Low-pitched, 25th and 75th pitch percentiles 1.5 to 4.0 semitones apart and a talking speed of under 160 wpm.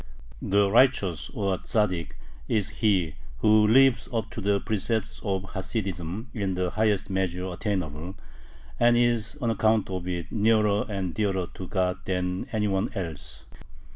Yes: low, 100 Hz; average, 3.0 semitones; average, 145 wpm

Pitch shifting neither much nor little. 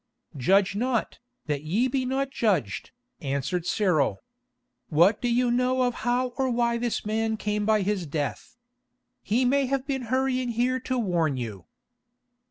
No: wide, 6.4 semitones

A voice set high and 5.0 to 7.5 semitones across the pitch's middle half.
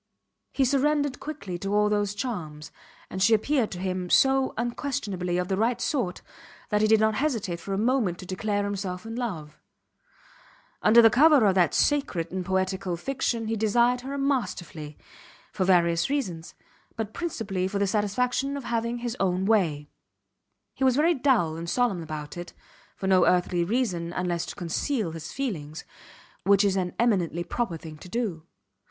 Yes: high, 200 Hz; wide, 5.4 semitones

